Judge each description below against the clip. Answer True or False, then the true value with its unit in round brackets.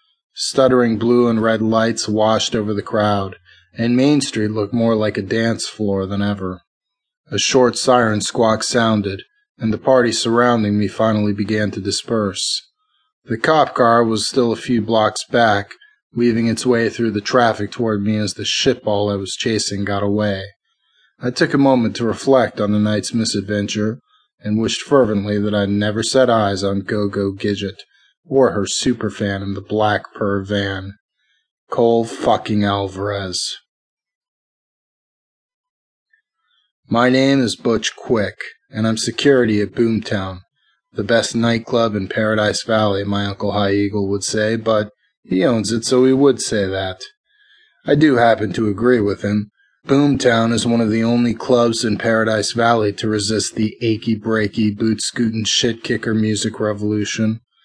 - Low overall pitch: True (110 Hz)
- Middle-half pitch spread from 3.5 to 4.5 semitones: False (2.6 semitones)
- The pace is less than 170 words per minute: True (160 wpm)